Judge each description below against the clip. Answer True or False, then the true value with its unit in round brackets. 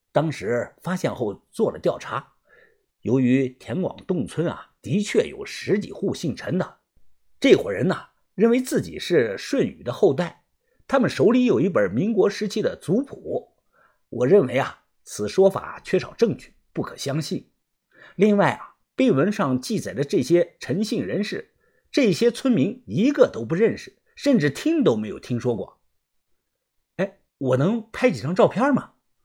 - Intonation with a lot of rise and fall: True (6.8 semitones)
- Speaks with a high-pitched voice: True (210 Hz)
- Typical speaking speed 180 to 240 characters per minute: True (230 characters per minute)